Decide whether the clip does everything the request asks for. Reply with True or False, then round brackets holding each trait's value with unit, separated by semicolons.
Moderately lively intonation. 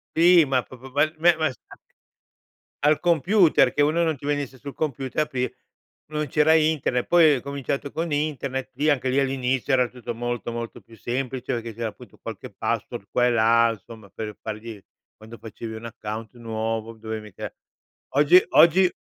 True (4.6 semitones)